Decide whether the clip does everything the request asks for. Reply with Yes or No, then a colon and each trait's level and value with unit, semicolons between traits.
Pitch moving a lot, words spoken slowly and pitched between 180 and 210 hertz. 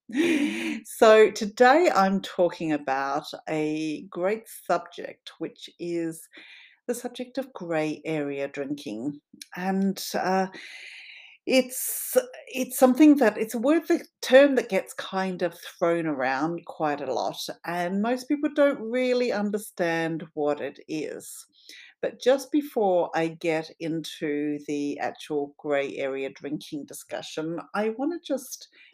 Yes: wide, 8.3 semitones; slow, 125 wpm; high, 190 Hz